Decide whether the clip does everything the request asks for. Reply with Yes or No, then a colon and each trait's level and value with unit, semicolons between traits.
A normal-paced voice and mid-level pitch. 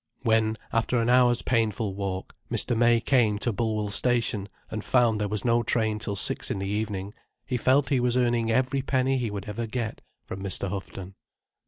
No: average, 190 wpm; low, 115 Hz